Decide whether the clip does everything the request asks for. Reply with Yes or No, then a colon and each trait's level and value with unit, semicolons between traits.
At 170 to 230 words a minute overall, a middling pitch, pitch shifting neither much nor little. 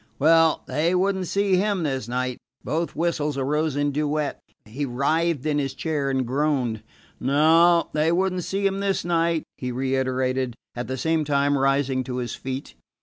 Yes: average, 175 wpm; medium, 145 Hz; average, 4.0 semitones